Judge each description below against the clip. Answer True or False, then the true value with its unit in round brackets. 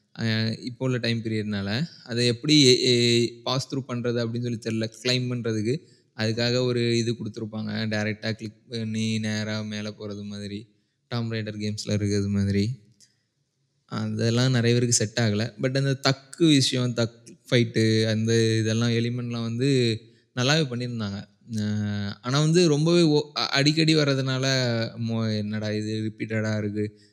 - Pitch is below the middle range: True (115 Hz)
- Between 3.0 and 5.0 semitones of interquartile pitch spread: False (2.6 semitones)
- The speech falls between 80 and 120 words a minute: False (130 wpm)